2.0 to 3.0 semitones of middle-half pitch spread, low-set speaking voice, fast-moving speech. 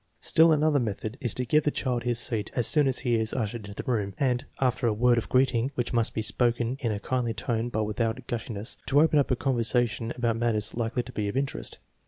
Yes: narrow, 2.4 semitones; low, 120 Hz; fast, 245 wpm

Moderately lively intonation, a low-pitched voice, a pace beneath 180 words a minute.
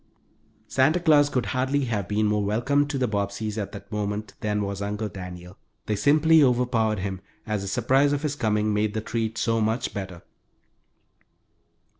Yes: average, 4.2 semitones; low, 110 Hz; average, 170 wpm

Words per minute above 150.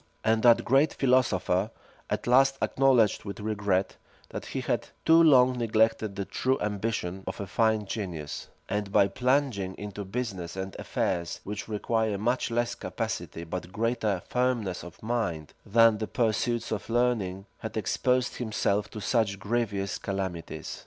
No: average, 145 wpm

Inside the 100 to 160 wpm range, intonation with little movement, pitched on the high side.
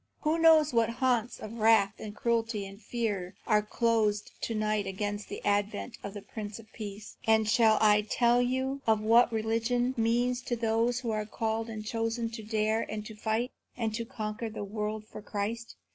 No: average, 185 wpm; narrow, 1.7 semitones; high, 220 Hz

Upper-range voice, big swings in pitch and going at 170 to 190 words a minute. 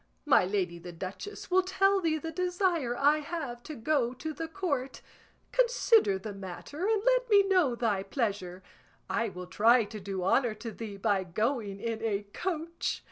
Yes: high, 245 Hz; wide, 9.0 semitones; average, 175 wpm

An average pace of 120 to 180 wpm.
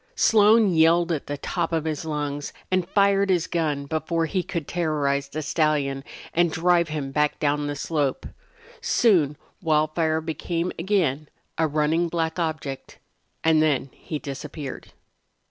Yes: average, 145 wpm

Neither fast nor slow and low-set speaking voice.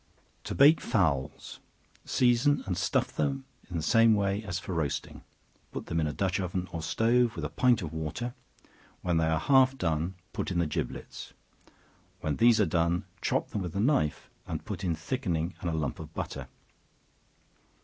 Yes: average, 175 wpm; very low, 90 Hz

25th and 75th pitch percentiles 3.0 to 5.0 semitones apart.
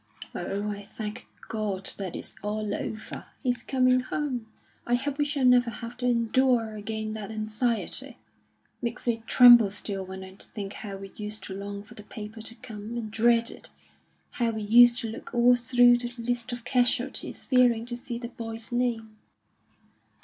No: narrow, 2.4 semitones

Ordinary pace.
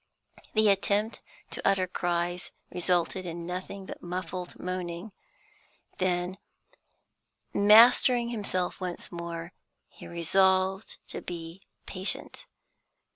No: slow, 95 wpm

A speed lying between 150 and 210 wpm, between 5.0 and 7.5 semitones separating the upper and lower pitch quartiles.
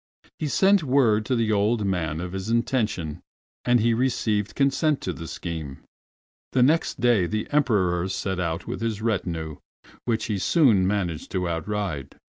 Yes: average, 160 wpm; average, 5.3 semitones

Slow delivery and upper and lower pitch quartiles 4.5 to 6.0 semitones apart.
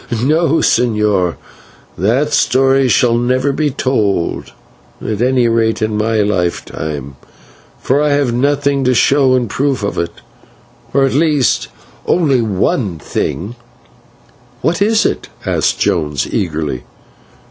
Yes: slow, 125 wpm; average, 5.2 semitones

